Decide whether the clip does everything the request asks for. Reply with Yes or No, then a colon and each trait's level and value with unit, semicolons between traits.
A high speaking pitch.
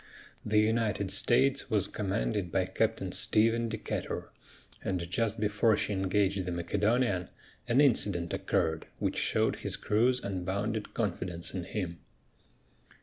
No: low, 105 Hz